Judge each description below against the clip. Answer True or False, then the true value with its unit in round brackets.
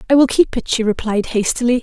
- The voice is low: False (240 Hz)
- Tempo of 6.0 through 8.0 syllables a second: True (6.1 syllables/s)